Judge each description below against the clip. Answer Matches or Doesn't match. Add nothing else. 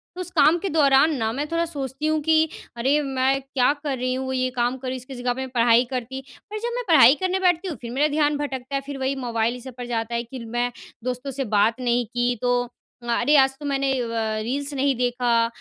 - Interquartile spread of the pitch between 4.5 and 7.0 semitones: Doesn't match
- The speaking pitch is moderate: Doesn't match